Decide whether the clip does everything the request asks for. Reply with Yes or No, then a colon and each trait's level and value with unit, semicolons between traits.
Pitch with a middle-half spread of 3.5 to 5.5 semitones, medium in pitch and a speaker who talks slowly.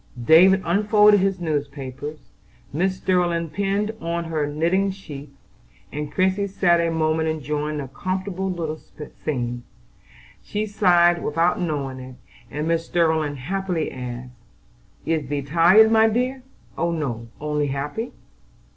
Yes: average, 4.3 semitones; medium, 165 Hz; slow, 130 wpm